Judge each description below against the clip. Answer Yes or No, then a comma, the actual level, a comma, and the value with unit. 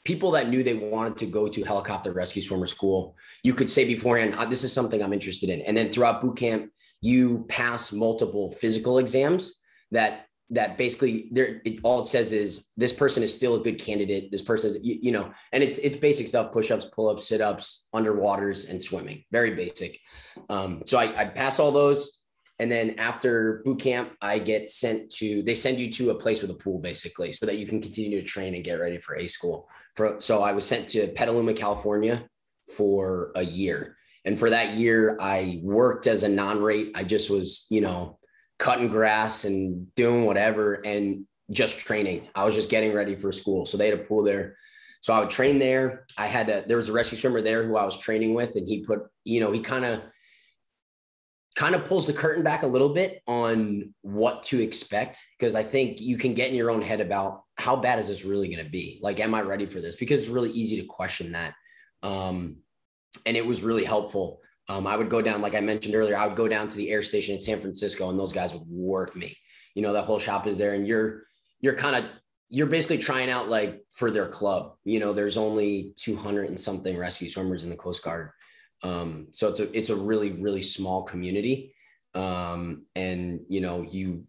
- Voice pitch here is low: Yes, low, 105 Hz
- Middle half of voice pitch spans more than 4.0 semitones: No, average, 3.0 semitones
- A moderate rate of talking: No, fast, 220 wpm